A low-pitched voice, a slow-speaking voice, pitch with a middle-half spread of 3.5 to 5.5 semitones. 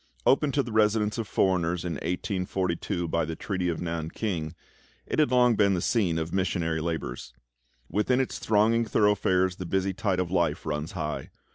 No: very low, 90 Hz; average, 175 wpm; average, 4.2 semitones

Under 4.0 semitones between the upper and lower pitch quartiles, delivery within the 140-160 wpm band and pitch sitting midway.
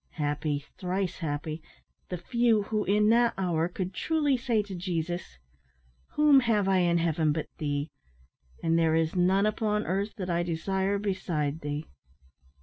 No: average, 4.3 semitones; average, 150 wpm; medium, 180 Hz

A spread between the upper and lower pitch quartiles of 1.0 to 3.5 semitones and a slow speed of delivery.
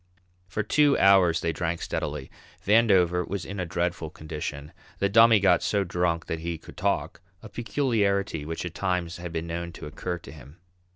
No: average, 3.2 semitones; average, 180 wpm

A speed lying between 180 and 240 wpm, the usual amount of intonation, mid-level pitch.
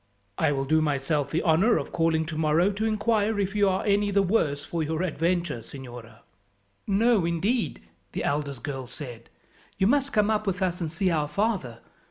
No: average, 185 wpm; wide, 5.7 semitones; medium, 170 Hz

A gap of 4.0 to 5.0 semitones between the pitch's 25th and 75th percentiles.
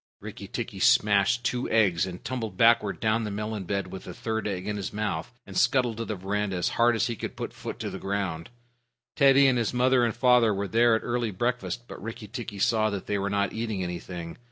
No: average, 3.1 semitones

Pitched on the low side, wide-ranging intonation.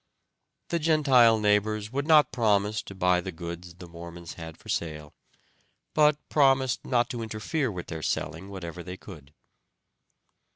Yes: low, 105 Hz; wide, 7.0 semitones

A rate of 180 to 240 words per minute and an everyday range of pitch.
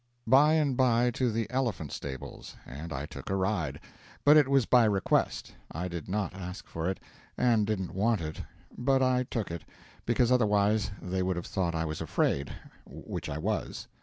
No: average, 185 wpm; wide, 6.3 semitones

